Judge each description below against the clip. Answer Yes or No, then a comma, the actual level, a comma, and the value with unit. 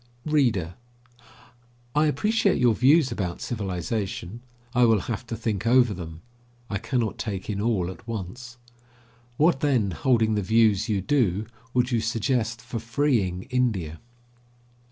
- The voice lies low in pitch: Yes, low, 115 Hz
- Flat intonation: No, average, 4.3 semitones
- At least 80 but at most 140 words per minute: Yes, slow, 135 wpm